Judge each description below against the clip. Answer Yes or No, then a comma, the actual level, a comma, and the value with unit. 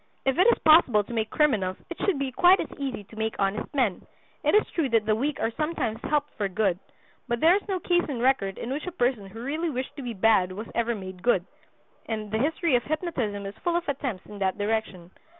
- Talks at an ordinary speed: No, fast, 240 wpm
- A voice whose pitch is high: Yes, high, 240 Hz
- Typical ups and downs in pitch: No, wide, 6.3 semitones